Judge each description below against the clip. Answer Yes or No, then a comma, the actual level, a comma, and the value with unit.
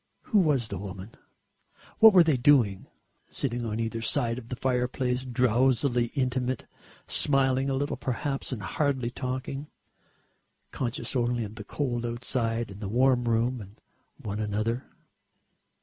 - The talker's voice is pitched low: Yes, low, 125 Hz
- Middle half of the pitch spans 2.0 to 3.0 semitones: Yes, narrow, 2.6 semitones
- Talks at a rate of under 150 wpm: Yes, average, 140 wpm